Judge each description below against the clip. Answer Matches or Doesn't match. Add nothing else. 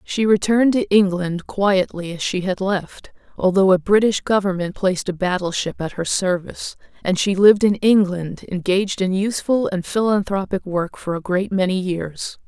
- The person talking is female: Matches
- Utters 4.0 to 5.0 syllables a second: Matches